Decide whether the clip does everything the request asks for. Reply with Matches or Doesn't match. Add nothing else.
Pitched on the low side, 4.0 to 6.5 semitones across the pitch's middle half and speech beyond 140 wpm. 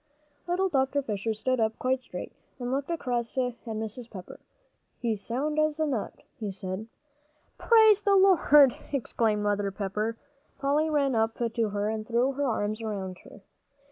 Doesn't match